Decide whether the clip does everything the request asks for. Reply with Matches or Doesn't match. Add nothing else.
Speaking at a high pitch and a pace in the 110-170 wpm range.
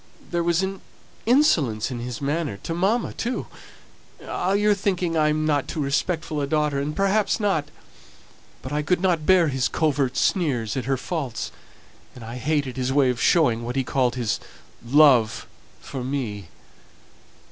Doesn't match